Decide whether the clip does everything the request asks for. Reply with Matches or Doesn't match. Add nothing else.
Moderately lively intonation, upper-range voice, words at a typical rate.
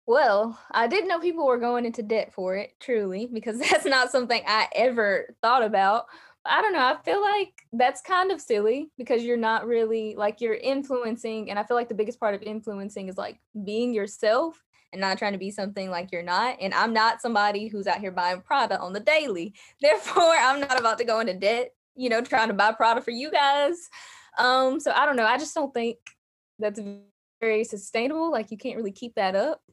Doesn't match